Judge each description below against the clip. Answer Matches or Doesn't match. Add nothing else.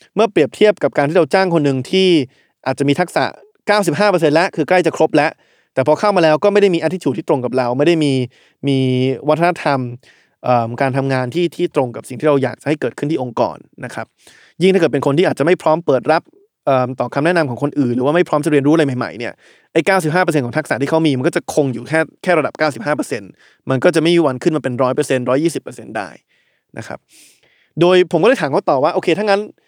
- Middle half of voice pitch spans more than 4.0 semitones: Matches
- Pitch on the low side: Doesn't match